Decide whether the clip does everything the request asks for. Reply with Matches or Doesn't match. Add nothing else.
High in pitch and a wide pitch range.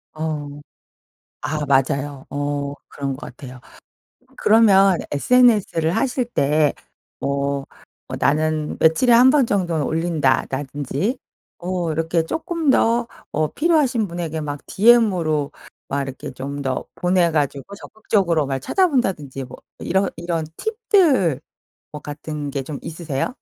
Doesn't match